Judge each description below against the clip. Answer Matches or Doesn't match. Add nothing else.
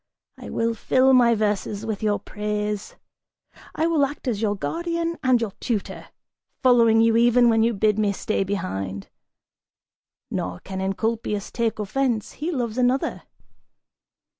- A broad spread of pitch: Doesn't match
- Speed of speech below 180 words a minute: Matches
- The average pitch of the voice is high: Matches